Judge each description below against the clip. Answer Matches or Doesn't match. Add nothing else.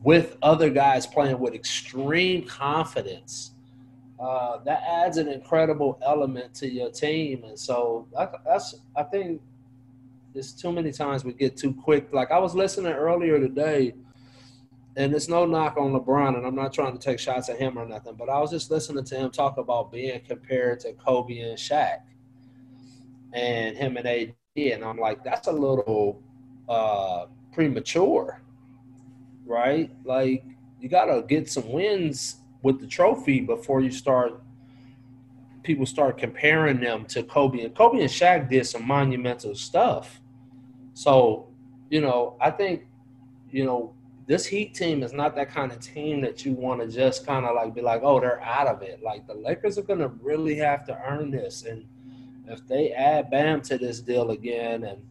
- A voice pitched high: Doesn't match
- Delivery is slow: Doesn't match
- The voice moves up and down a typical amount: Doesn't match